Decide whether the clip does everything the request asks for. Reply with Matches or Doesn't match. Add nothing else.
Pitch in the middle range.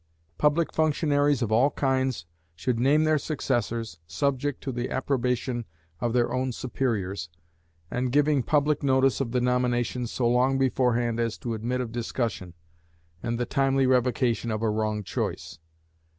Doesn't match